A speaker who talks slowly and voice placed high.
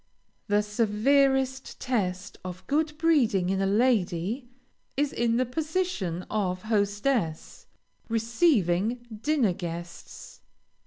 Yes: slow, 100 wpm; high, 220 Hz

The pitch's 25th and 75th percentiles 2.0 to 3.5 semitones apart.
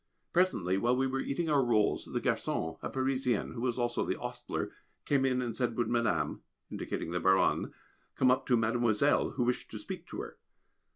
Yes: average, 2.7 semitones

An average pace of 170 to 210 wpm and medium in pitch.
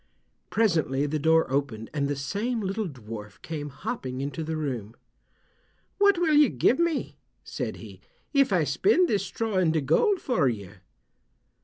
No: average, 155 wpm; medium, 160 Hz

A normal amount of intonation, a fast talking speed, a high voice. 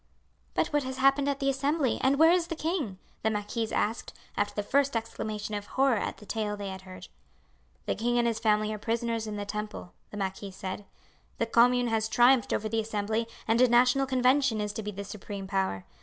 Yes: average, 3.7 semitones; fast, 215 wpm; high, 225 Hz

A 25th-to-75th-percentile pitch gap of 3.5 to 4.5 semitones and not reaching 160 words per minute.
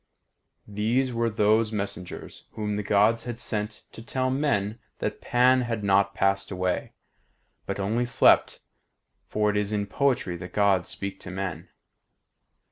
No: average, 2.9 semitones; average, 145 wpm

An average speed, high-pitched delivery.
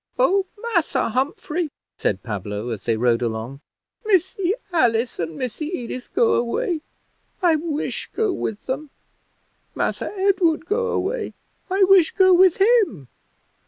No: slow, 130 wpm; very high, 315 Hz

